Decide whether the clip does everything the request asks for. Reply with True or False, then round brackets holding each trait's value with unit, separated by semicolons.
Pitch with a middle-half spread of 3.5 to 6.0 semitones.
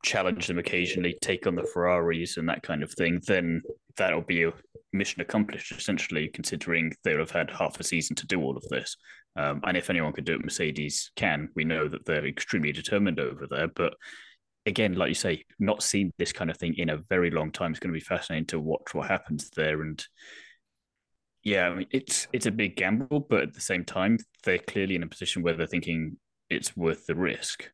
False (2.7 semitones)